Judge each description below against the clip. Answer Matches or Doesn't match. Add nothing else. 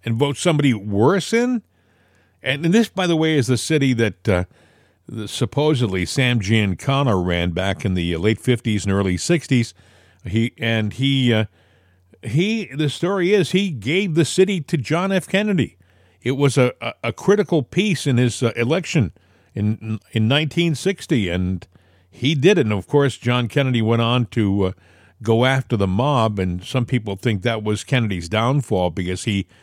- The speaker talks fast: Doesn't match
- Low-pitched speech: Matches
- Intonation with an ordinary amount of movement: Doesn't match